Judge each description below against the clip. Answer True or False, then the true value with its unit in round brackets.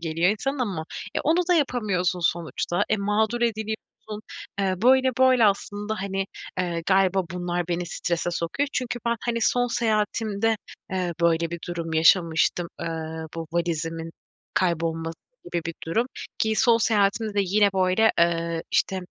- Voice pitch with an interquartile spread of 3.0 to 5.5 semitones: True (4.5 semitones)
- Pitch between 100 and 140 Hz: False (195 Hz)